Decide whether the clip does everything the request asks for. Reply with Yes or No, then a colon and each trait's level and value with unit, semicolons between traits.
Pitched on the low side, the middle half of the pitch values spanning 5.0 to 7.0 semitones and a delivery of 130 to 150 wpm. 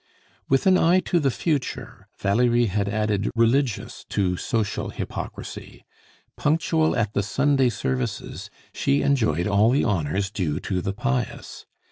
Yes: low, 115 Hz; wide, 5.6 semitones; slow, 135 wpm